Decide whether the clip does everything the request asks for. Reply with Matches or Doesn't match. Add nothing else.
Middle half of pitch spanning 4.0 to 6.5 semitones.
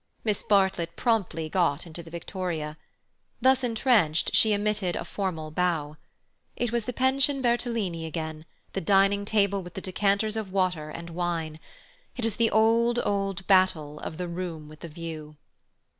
Matches